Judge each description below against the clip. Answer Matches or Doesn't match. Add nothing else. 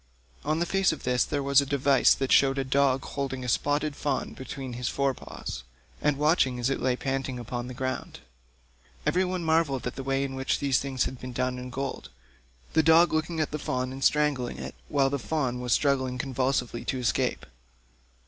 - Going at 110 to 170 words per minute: Doesn't match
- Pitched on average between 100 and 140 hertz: Matches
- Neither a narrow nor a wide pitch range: Doesn't match